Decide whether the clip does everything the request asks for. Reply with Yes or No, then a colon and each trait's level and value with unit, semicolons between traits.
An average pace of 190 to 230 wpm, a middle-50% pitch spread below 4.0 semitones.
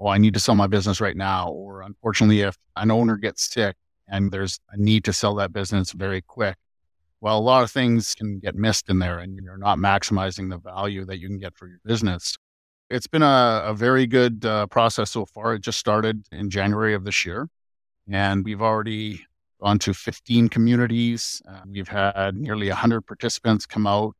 Yes: fast, 205 wpm; narrow, 2.4 semitones